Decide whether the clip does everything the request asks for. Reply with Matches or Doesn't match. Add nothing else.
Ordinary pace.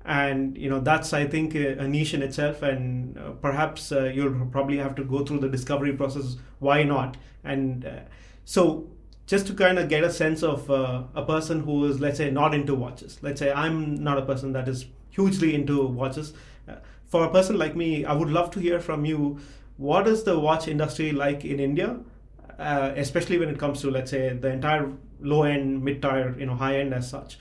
Doesn't match